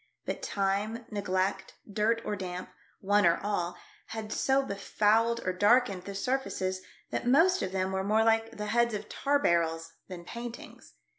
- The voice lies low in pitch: No, high, 205 Hz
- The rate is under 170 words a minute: No, average, 175 wpm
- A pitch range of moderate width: Yes, average, 3.4 semitones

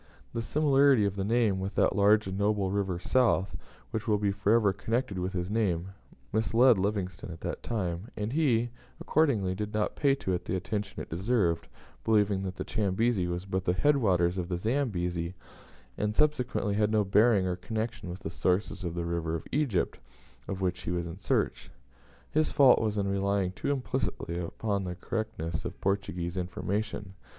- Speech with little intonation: No, average, 3.6 semitones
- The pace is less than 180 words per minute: No, average, 185 wpm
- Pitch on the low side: Yes, low, 100 Hz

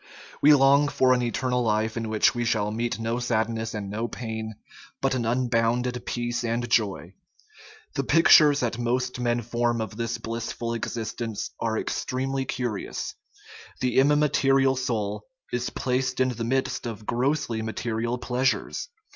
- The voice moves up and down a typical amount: No, narrow, 2.1 semitones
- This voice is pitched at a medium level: No, low, 120 Hz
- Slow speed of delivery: No, average, 150 wpm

